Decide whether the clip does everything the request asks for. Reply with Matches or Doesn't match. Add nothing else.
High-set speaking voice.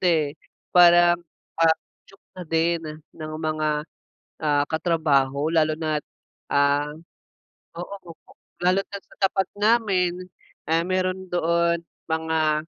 Doesn't match